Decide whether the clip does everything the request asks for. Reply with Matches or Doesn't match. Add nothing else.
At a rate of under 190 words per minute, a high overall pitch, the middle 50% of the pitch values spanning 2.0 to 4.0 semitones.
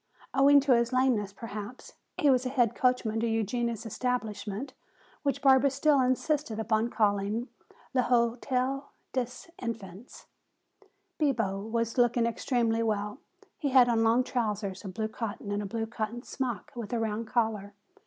Matches